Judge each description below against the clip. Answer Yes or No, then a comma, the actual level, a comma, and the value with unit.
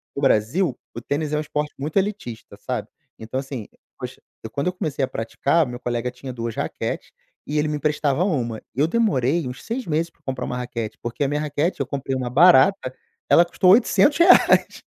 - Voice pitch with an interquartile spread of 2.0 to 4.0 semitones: No, average, 5.1 semitones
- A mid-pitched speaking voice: Yes, medium, 145 Hz